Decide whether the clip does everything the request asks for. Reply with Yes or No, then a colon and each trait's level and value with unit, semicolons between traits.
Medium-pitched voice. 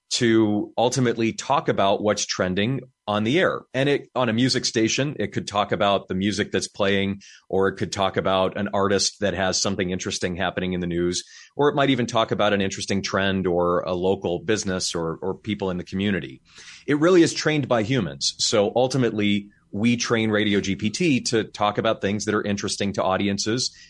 No: low, 105 Hz